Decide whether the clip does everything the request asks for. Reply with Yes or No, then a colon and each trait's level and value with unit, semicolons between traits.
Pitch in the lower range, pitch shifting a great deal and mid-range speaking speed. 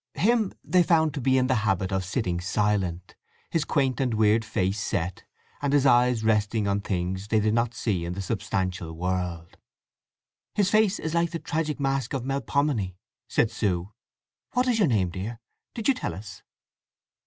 Yes: low, 110 Hz; wide, 6.9 semitones; average, 175 wpm